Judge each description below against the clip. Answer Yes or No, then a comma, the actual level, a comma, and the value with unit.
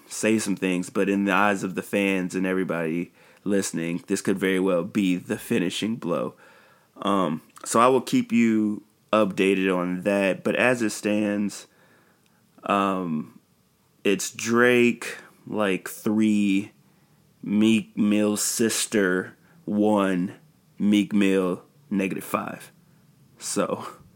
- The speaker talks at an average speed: No, slow, 120 wpm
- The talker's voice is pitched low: Yes, low, 100 Hz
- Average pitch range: No, narrow, 2.1 semitones